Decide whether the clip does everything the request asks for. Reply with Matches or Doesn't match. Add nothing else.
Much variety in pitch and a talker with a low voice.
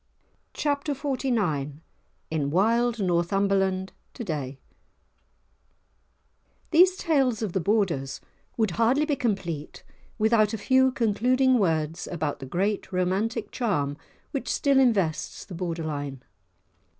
Doesn't match